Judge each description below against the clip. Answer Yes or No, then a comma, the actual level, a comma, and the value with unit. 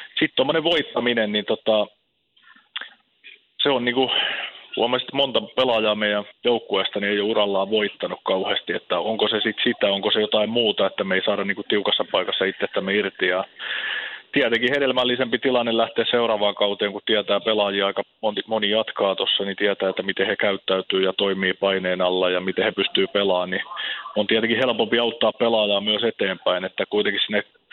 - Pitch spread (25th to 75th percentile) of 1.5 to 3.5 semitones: Yes, average, 2.9 semitones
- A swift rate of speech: Yes, fast, 175 wpm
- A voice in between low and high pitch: No, low, 105 Hz